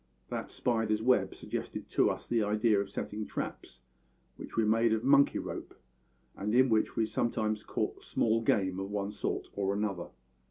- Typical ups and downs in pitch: No, narrow, 1.9 semitones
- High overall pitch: No, low, 110 Hz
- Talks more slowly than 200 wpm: Yes, average, 170 wpm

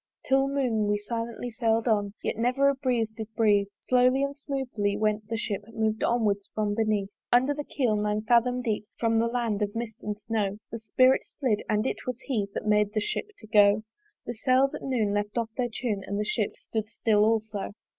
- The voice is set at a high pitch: Yes, high, 225 Hz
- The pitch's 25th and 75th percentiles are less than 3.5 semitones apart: Yes, average, 2.9 semitones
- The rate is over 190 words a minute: Yes, fast, 205 wpm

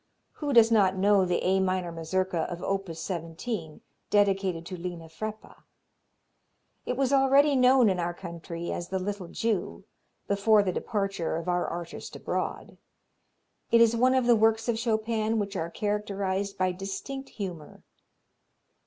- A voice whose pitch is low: No, high, 195 Hz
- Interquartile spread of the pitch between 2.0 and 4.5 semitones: Yes, average, 4.0 semitones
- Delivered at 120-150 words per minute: Yes, average, 145 wpm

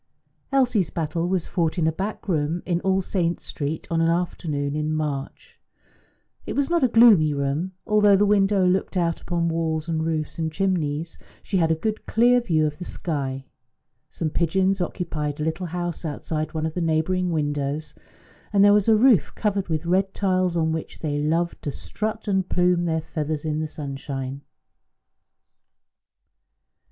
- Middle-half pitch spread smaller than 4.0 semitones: Yes, average, 3.6 semitones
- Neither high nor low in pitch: Yes, medium, 165 Hz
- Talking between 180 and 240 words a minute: No, average, 170 wpm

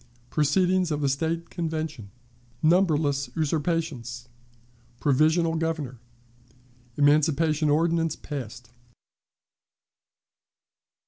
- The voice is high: No, medium, 155 Hz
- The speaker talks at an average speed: No, slow, 65 wpm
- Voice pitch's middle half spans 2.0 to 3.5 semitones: Yes, average, 2.7 semitones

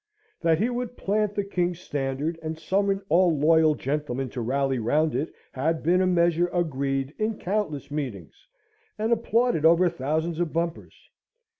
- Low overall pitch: No, medium, 165 Hz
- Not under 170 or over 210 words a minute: No, average, 155 wpm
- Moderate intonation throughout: Yes, average, 4.4 semitones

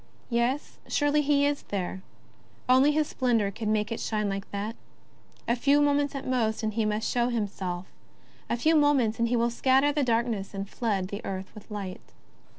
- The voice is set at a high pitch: Yes, high, 235 Hz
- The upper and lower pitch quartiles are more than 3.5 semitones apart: Yes, average, 4.8 semitones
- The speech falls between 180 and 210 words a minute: Yes, average, 185 wpm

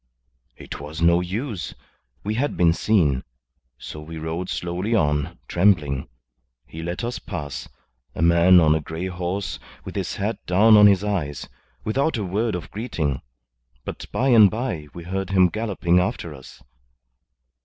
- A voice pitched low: Yes, very low, 90 Hz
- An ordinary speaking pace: Yes, average, 155 wpm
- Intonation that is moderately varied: Yes, average, 4.4 semitones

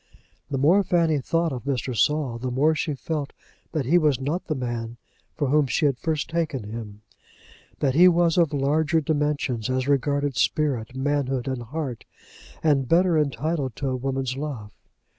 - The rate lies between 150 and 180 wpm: Yes, average, 170 wpm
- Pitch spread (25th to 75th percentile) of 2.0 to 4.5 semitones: Yes, average, 3.3 semitones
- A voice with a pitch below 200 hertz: Yes, medium, 140 Hz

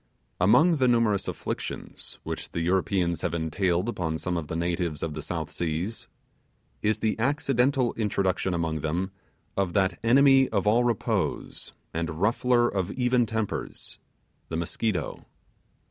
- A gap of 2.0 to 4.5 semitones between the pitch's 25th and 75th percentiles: No, wide, 5.6 semitones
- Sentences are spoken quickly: No, average, 140 wpm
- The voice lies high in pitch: No, very low, 95 Hz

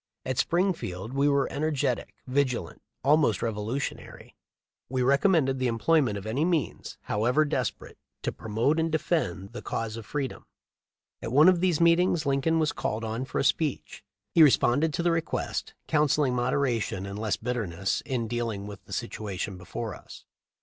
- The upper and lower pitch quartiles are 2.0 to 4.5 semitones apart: No, wide, 5.5 semitones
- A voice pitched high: No, low, 130 Hz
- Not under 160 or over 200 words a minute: Yes, average, 170 wpm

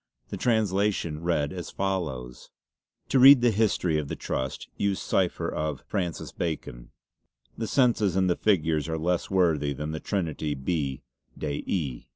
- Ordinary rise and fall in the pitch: Yes, average, 4.6 semitones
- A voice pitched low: Yes, very low, 85 Hz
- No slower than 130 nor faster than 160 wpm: Yes, average, 155 wpm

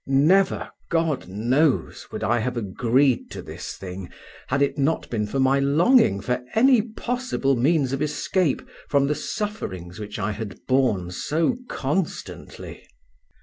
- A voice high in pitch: No, low, 135 Hz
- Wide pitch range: Yes, wide, 6.5 semitones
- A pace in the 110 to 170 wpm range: Yes, average, 145 wpm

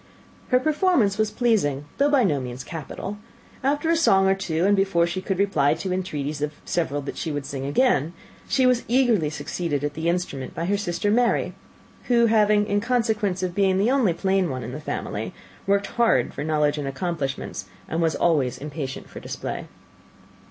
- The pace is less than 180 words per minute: No, average, 185 wpm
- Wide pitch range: Yes, wide, 6.3 semitones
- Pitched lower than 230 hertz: Yes, medium, 185 Hz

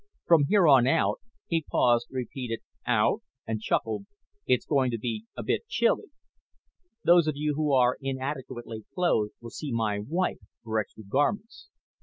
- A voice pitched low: Yes, low, 130 Hz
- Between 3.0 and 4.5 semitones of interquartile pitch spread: No, average, 5.2 semitones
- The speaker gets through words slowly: No, average, 160 wpm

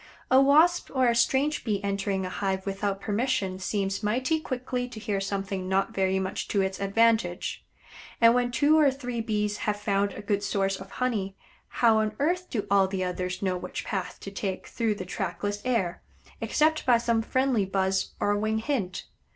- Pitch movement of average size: Yes, average, 4.1 semitones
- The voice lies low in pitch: No, high, 205 Hz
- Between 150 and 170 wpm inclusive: No, average, 185 wpm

